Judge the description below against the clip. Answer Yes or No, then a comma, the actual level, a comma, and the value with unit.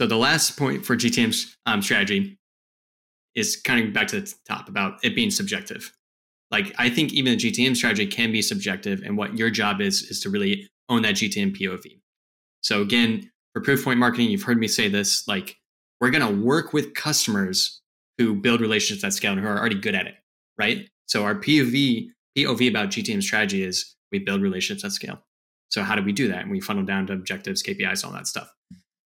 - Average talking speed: No, fast, 210 wpm